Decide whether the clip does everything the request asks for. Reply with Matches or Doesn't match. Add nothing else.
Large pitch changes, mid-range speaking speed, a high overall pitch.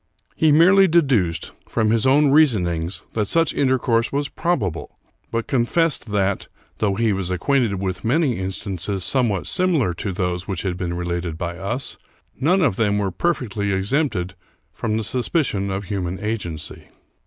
Doesn't match